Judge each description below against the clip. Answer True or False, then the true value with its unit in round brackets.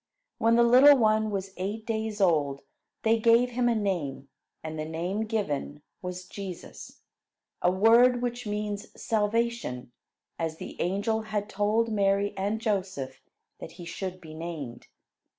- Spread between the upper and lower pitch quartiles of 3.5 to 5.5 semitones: True (4.3 semitones)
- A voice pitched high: True (205 Hz)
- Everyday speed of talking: True (150 wpm)